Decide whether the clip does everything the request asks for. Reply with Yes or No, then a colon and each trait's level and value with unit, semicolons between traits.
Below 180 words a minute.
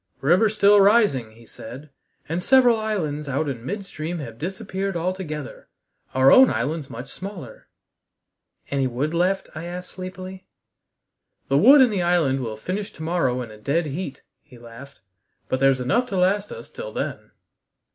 Yes: average, 160 wpm